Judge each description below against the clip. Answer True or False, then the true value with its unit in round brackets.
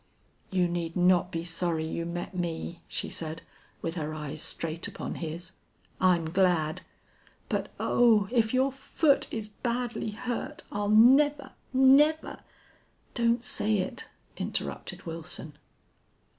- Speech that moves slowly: True (130 wpm)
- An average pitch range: False (6.5 semitones)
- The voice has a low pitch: False (185 Hz)